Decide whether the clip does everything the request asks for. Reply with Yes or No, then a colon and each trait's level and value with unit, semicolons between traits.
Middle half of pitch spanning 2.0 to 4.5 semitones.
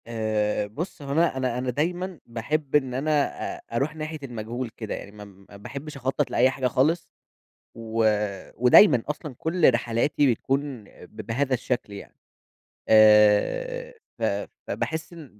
No: average, 5.2 semitones